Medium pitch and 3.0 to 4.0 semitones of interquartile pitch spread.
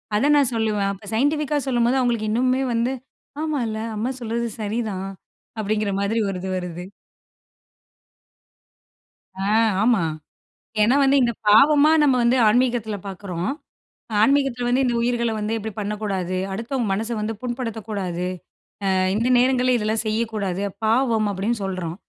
No: high, 225 Hz; average, 3.4 semitones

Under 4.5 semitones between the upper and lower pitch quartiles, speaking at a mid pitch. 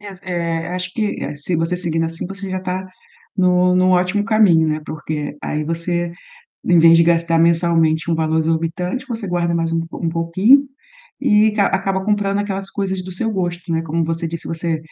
Yes: narrow, 2.5 semitones; medium, 175 Hz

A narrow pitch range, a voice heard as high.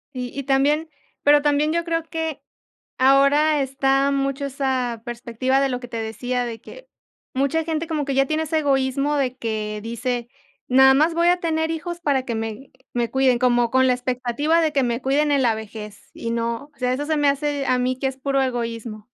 No: average, 3.2 semitones; very high, 270 Hz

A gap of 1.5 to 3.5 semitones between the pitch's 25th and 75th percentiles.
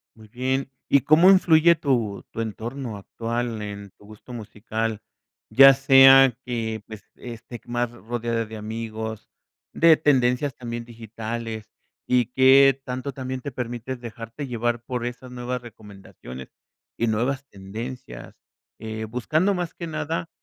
Yes: average, 3.1 semitones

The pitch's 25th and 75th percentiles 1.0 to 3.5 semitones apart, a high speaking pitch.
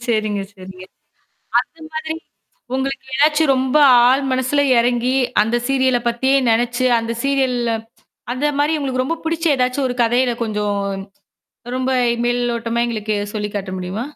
Yes: average, 2.9 semitones; very high, 250 Hz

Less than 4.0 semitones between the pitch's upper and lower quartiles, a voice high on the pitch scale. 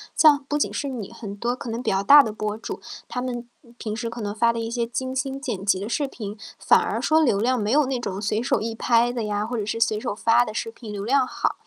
Yes: average, 3.2 semitones; high, 230 Hz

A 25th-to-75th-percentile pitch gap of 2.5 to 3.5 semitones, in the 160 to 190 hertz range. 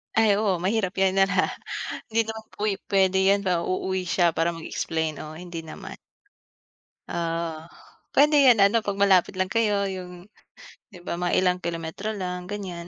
Yes: average, 2.8 semitones; medium, 185 Hz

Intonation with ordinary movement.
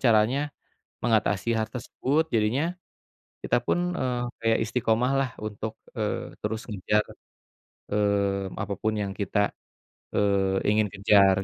Yes: average, 3.3 semitones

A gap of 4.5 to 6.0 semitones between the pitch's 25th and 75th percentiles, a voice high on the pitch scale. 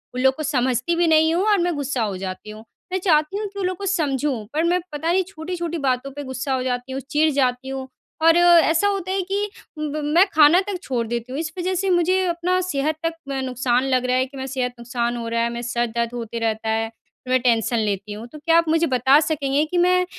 Yes: wide, 5.6 semitones; very high, 280 Hz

